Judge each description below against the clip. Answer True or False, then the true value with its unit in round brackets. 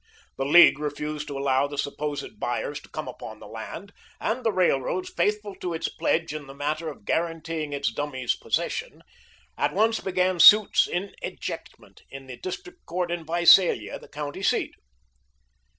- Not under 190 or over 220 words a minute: False (165 wpm)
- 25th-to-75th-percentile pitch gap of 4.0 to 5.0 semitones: True (4.5 semitones)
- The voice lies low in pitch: False (160 Hz)